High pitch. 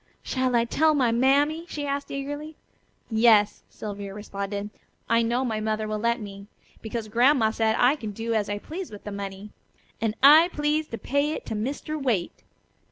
Yes: high, 230 Hz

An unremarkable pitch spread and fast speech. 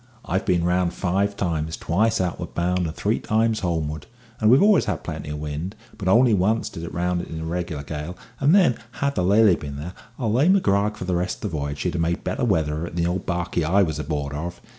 Yes: average, 4.1 semitones; fast, 250 wpm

